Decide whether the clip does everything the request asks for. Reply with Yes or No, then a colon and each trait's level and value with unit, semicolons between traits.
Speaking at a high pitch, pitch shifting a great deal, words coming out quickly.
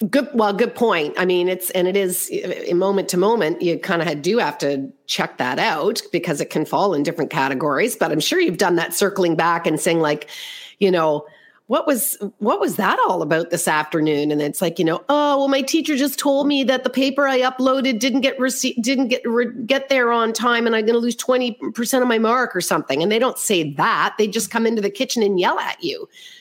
Yes: high, 235 Hz; wide, 6.6 semitones; fast, 235 wpm